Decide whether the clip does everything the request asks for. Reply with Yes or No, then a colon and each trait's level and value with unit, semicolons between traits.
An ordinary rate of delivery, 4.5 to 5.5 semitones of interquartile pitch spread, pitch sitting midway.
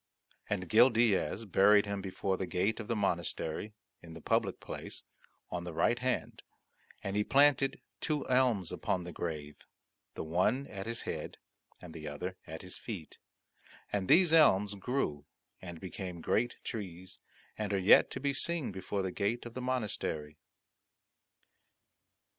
No: average, 155 wpm; average, 5.0 semitones; low, 100 Hz